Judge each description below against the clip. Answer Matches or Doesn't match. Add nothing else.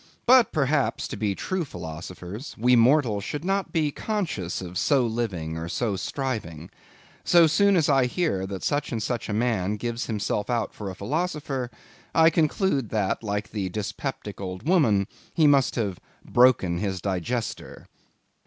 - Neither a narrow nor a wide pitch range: Doesn't match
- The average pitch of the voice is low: Matches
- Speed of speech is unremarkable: Matches